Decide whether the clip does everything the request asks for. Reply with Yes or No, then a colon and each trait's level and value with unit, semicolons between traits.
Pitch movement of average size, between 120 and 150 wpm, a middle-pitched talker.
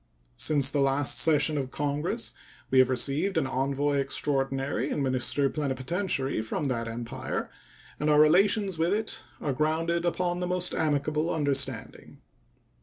Yes: average, 3.5 semitones; average, 140 wpm; medium, 145 Hz